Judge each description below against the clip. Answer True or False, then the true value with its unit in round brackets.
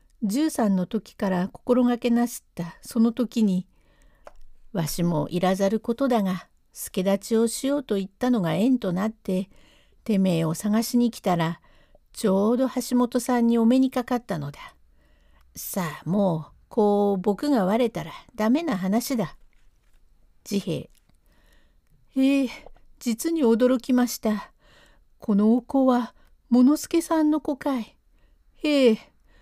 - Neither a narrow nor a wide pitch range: True (4.9 semitones)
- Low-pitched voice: False (225 Hz)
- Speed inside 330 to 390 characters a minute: False (240 characters per minute)